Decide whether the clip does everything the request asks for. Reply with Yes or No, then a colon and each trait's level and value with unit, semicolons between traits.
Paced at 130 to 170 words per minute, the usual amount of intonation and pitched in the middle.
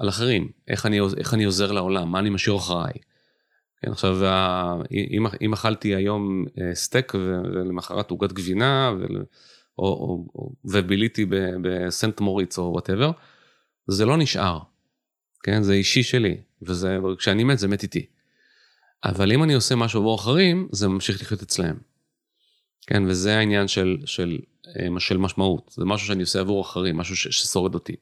No: fast, 150 wpm; average, 3.2 semitones; low, 100 Hz